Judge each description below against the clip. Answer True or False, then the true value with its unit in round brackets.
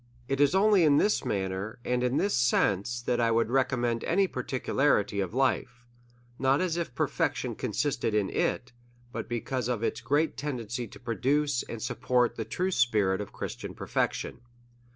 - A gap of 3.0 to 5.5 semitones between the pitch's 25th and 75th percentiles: True (3.4 semitones)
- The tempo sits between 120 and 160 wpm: False (170 wpm)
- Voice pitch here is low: True (125 Hz)